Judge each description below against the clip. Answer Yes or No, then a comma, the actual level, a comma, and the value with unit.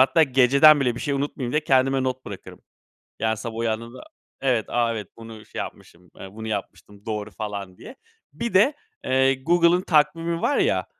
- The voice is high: No, low, 130 Hz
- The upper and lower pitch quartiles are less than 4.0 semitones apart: No, average, 5.2 semitones